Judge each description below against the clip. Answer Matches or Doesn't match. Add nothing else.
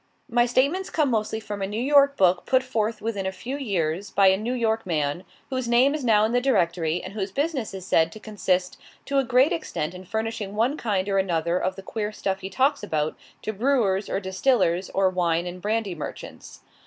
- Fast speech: Matches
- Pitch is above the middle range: Matches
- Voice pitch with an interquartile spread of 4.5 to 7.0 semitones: Matches